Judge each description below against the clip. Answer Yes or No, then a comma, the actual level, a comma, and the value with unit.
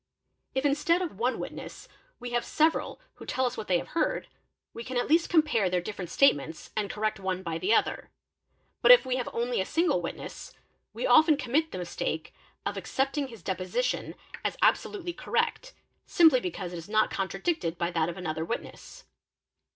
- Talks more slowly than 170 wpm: No, average, 185 wpm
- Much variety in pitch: Yes, wide, 8.4 semitones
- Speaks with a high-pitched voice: Yes, high, 235 Hz